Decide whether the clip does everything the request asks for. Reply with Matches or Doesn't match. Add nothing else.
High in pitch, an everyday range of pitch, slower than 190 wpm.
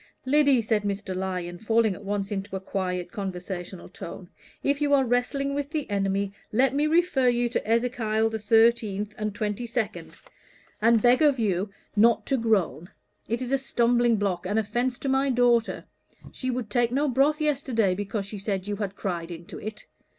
Matches